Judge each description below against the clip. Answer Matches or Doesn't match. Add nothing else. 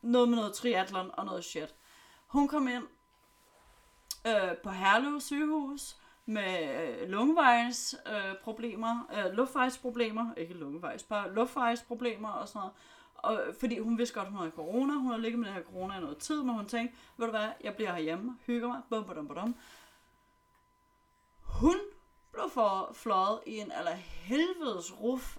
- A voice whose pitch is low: Doesn't match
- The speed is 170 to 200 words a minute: Doesn't match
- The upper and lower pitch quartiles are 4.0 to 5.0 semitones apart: Doesn't match